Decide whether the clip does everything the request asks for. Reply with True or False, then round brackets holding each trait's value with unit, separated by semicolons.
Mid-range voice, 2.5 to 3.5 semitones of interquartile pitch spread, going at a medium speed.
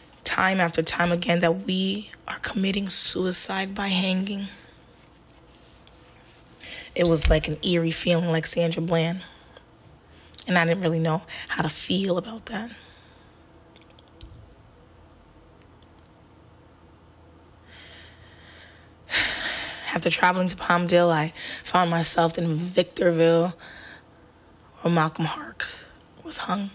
False (170 Hz; 2.9 semitones; 100 wpm)